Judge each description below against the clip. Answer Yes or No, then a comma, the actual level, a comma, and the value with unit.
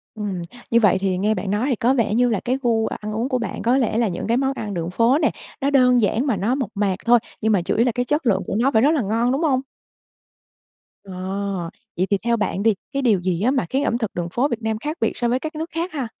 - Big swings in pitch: No, average, 3.8 semitones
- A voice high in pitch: Yes, high, 235 Hz